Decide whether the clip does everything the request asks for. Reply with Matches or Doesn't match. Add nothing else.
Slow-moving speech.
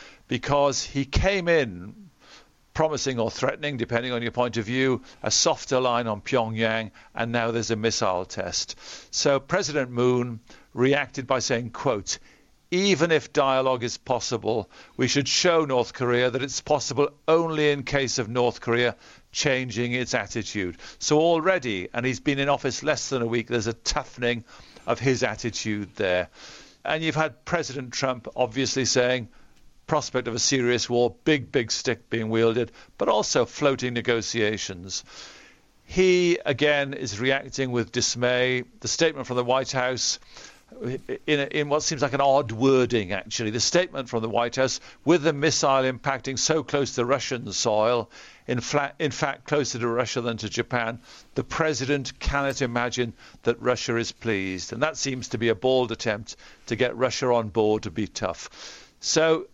Doesn't match